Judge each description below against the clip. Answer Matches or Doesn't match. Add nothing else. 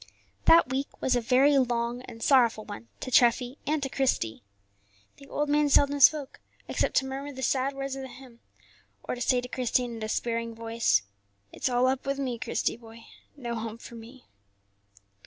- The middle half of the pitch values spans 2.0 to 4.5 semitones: Matches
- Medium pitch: Doesn't match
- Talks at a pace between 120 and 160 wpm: Doesn't match